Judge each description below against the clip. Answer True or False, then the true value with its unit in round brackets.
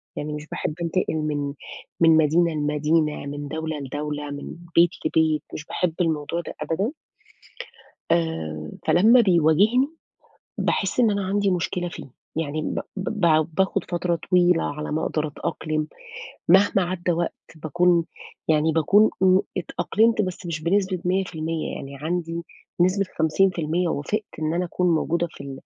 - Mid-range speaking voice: True (165 Hz)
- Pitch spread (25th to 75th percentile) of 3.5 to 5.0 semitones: False (3.0 semitones)